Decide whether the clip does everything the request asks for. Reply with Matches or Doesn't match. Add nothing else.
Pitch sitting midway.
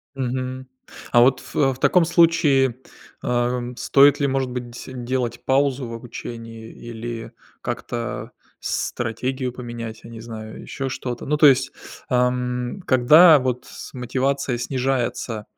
Doesn't match